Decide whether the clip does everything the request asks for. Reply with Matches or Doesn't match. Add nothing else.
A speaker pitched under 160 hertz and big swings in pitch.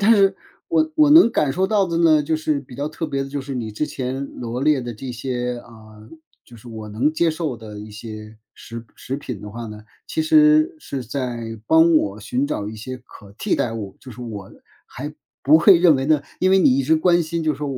Matches